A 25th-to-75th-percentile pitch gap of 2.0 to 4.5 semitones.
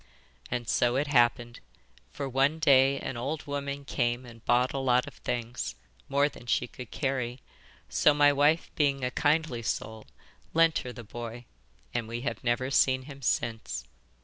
Yes: average, 2.8 semitones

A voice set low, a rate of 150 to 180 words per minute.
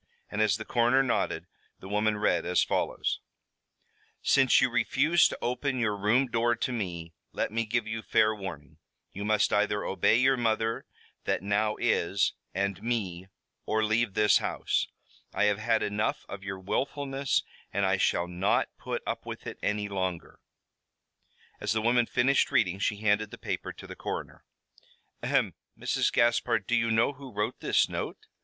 Yes: low, 110 Hz; average, 170 wpm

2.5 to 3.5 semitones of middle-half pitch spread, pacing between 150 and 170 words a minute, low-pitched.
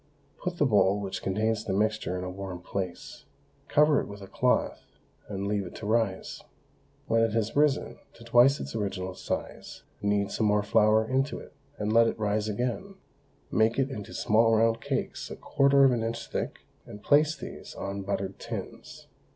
No: average, 2.8 semitones; average, 185 wpm; low, 110 Hz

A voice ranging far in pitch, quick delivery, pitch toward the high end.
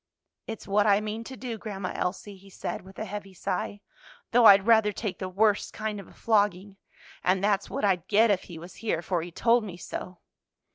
No: narrow, 2.4 semitones; fast, 210 wpm; high, 200 Hz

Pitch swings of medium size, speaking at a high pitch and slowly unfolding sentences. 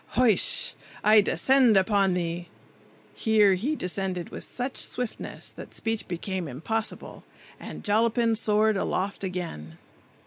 Yes: average, 3.6 semitones; high, 205 Hz; slow, 115 wpm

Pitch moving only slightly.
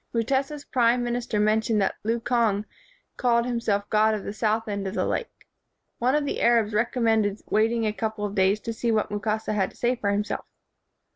Yes: narrow, 2.2 semitones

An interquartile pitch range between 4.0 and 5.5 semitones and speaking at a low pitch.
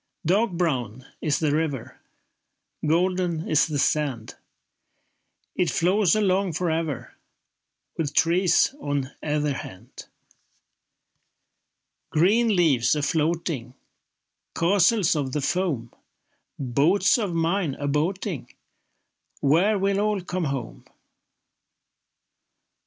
No: average, 4.5 semitones; medium, 165 Hz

